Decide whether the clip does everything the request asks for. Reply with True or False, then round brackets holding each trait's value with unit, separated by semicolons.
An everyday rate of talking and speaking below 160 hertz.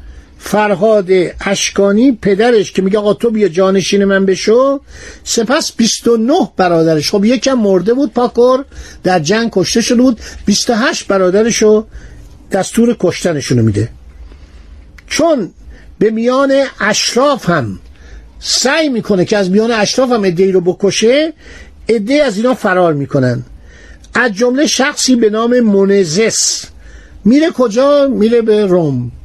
False (125 wpm; 205 Hz)